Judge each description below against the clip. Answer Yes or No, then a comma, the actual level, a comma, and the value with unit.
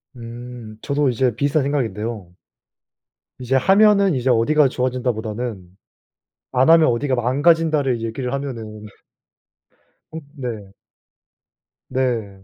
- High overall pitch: No, low, 125 Hz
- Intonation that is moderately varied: Yes, average, 3.7 semitones